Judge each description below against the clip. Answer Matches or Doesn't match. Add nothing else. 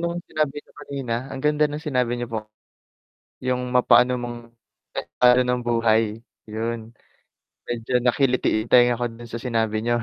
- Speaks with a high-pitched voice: Doesn't match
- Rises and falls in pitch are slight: Matches